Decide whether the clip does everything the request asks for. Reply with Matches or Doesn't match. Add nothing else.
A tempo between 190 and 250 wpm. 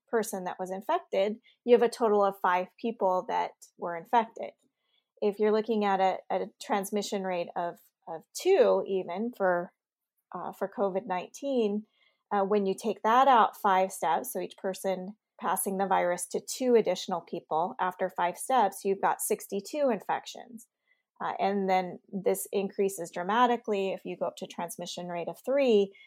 Doesn't match